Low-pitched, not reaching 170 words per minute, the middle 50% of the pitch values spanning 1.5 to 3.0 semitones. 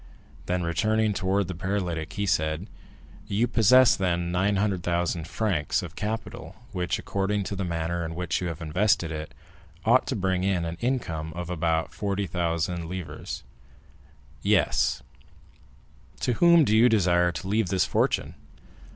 No: very low, 90 Hz; average, 140 wpm; average, 3.4 semitones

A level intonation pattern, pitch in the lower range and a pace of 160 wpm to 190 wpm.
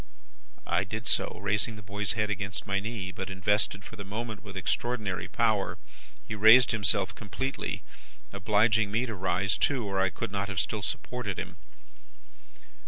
Yes: narrow, 2.2 semitones; low, 105 Hz; average, 165 wpm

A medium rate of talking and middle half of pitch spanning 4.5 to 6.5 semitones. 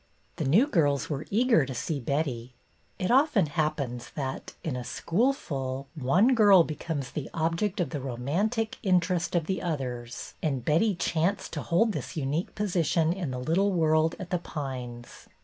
Yes: average, 170 wpm; wide, 5.4 semitones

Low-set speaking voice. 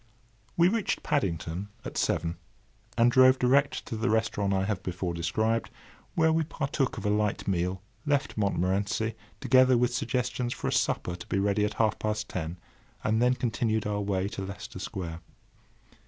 Yes: low, 110 Hz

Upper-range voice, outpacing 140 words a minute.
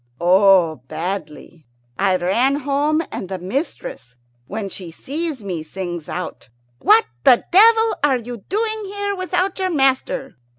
No: high, 245 Hz; slow, 135 wpm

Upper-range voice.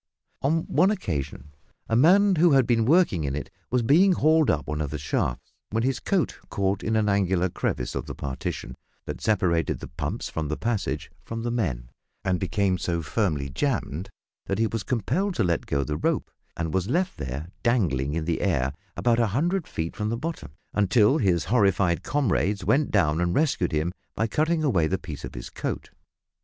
No: low, 100 Hz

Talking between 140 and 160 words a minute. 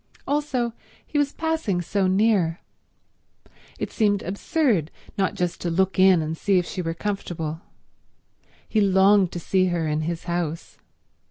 Yes: average, 150 wpm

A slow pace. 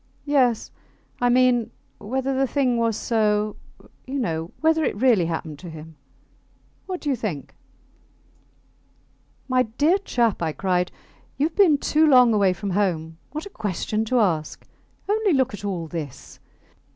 No: average, 150 wpm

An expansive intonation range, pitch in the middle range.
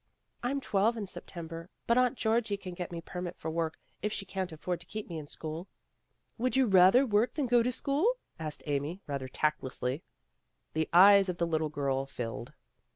Yes: wide, 5.8 semitones; medium, 180 Hz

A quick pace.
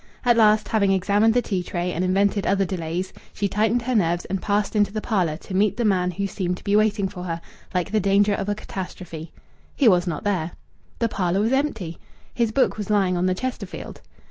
Yes: fast, 220 wpm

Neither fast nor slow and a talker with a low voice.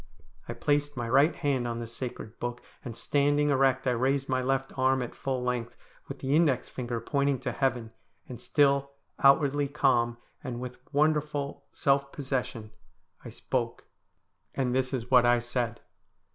Yes: average, 160 wpm; low, 130 Hz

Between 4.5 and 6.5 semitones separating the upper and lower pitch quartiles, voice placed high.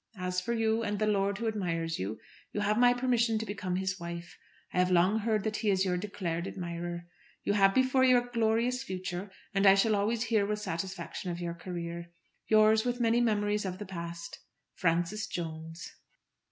No: average, 4.0 semitones; high, 200 Hz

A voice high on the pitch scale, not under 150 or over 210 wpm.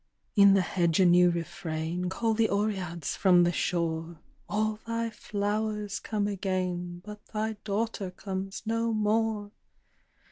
No: high, 200 Hz; slow, 135 wpm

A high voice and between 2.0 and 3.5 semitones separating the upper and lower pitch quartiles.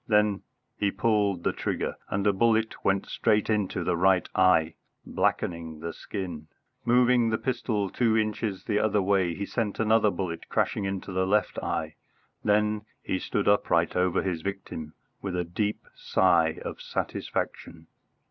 No: low, 100 Hz; average, 3.0 semitones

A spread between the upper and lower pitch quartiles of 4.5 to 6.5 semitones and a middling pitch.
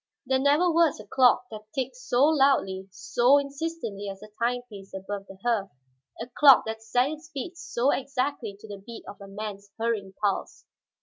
No: wide, 5.4 semitones; high, 240 Hz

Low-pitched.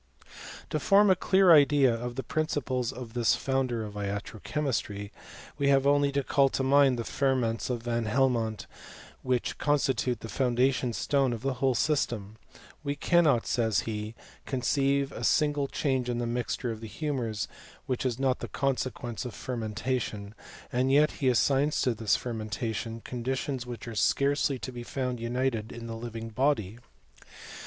Yes: low, 125 Hz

